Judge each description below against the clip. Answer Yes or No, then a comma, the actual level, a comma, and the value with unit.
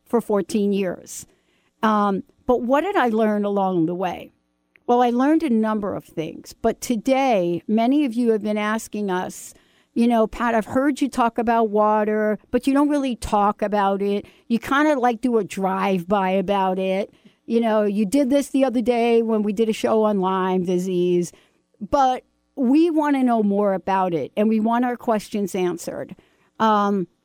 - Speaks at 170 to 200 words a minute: Yes, average, 185 wpm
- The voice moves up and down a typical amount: Yes, average, 3.8 semitones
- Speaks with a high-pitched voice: Yes, high, 220 Hz